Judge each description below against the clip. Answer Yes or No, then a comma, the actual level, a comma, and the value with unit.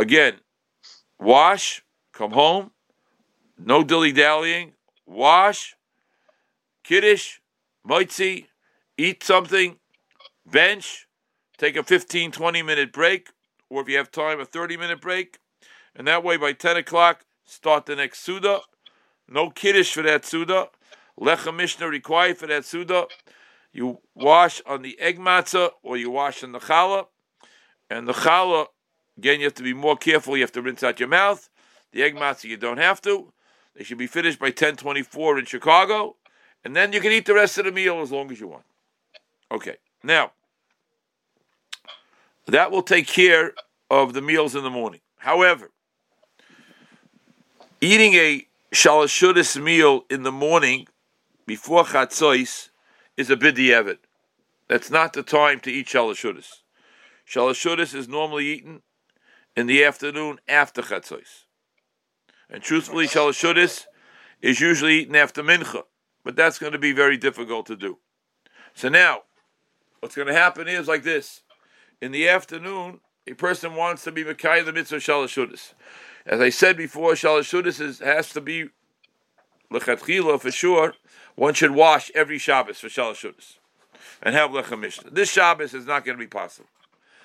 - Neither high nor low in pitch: Yes, medium, 160 Hz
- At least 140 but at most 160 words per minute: Yes, average, 150 wpm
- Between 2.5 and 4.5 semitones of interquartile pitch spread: Yes, average, 4.0 semitones